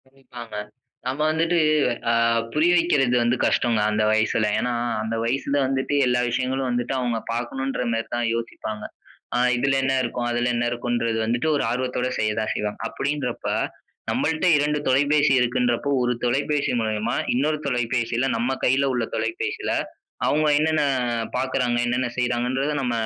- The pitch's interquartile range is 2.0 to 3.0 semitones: Yes, narrow, 2.5 semitones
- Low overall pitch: Yes, low, 125 Hz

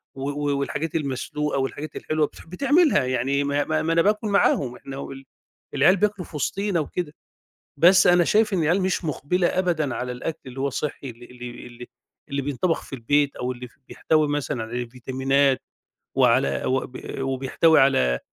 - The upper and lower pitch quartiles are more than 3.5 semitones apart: Yes, average, 4.1 semitones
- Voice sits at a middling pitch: Yes, medium, 145 Hz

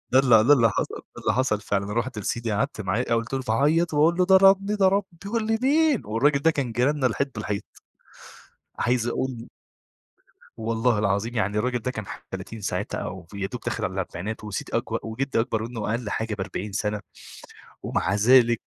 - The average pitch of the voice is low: Yes, low, 120 Hz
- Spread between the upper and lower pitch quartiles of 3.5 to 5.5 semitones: Yes, average, 4.7 semitones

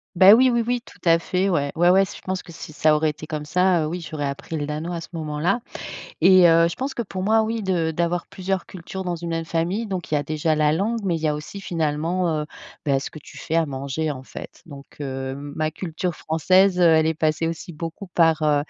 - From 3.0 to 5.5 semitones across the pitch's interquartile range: Yes, average, 3.3 semitones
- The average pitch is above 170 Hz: No, medium, 165 Hz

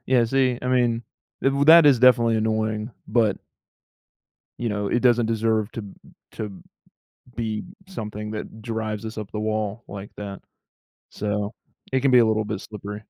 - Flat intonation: Yes, narrow, 2.2 semitones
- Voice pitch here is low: Yes, low, 110 Hz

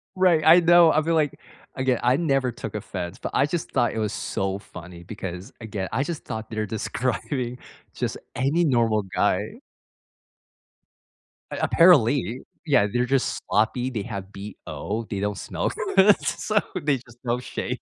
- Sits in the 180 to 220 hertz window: No, low, 120 Hz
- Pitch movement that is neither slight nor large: No, wide, 5.9 semitones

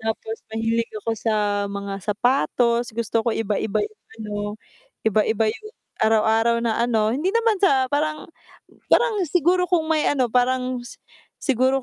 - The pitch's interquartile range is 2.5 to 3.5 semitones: No, average, 4.2 semitones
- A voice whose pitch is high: Yes, high, 235 Hz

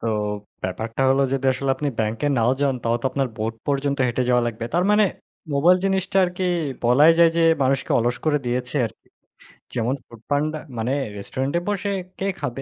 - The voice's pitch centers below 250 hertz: Yes, low, 135 Hz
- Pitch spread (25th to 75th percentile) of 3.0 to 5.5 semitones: Yes, average, 4.5 semitones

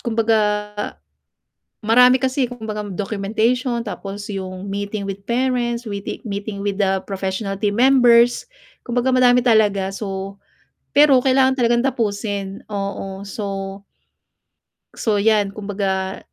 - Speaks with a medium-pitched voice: No, high, 210 Hz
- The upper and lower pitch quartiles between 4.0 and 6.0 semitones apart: No, average, 3.4 semitones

